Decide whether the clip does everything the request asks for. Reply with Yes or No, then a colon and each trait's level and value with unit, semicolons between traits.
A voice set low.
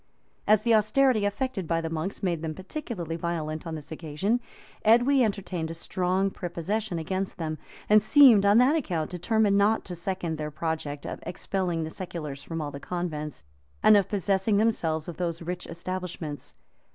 No: medium, 180 Hz